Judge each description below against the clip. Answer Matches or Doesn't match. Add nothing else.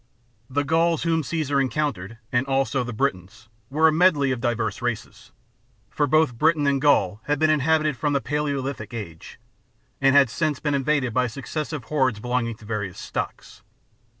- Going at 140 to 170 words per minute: Matches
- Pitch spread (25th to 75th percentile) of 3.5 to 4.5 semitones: Matches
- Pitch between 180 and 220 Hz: Doesn't match